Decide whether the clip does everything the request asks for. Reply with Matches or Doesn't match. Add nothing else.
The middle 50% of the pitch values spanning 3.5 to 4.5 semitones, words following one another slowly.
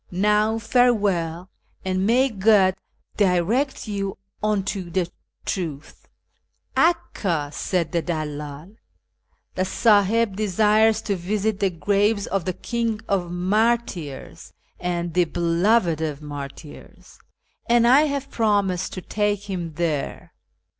Matches